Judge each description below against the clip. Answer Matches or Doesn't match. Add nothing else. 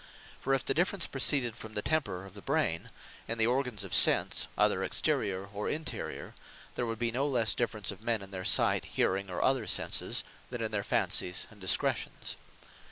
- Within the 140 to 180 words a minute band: Doesn't match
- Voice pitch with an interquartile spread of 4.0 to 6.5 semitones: Matches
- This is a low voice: Matches